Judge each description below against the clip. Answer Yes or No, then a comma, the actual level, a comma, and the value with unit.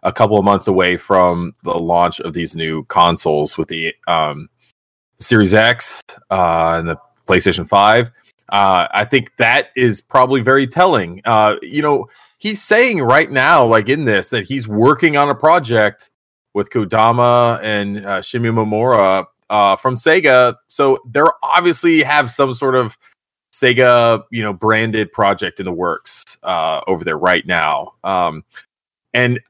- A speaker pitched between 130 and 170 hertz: No, low, 115 Hz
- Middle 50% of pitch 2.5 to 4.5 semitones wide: No, wide, 5.4 semitones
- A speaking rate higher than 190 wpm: No, average, 155 wpm